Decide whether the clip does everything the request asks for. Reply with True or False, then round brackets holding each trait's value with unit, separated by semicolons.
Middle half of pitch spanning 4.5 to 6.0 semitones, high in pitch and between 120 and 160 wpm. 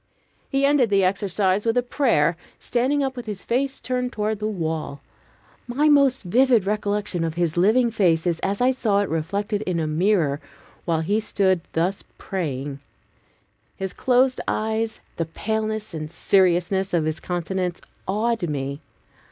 True (5.2 semitones; 200 Hz; 155 wpm)